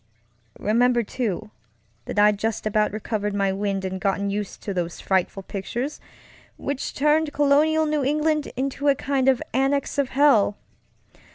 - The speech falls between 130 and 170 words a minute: Yes, average, 150 wpm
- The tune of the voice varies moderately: No, wide, 5.8 semitones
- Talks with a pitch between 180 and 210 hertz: No, high, 235 Hz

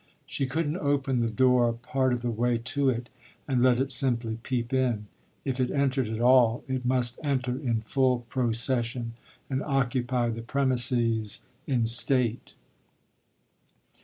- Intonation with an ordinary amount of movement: No, narrow, 2.0 semitones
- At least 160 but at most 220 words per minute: No, average, 150 wpm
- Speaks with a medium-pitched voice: No, low, 125 Hz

